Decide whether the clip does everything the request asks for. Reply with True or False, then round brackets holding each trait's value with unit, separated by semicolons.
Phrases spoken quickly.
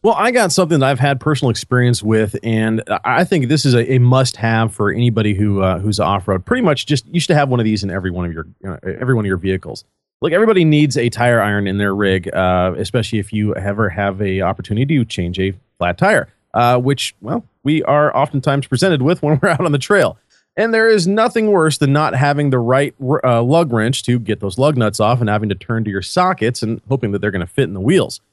True (250 wpm)